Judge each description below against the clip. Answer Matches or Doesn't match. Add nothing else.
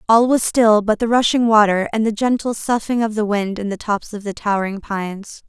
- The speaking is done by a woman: Matches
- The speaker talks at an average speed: Doesn't match